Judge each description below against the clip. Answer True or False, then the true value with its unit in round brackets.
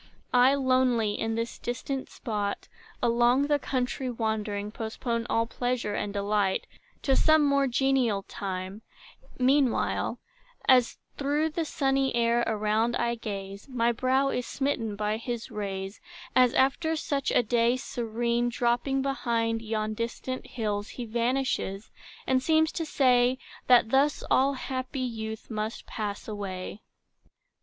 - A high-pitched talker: True (240 Hz)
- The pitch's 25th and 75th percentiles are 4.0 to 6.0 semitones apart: False (3.3 semitones)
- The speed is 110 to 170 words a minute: True (135 wpm)